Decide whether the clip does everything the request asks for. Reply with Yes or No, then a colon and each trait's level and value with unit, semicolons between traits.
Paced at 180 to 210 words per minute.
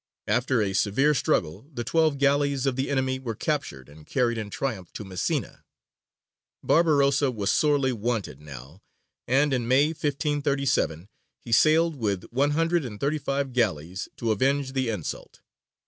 No: average, 150 wpm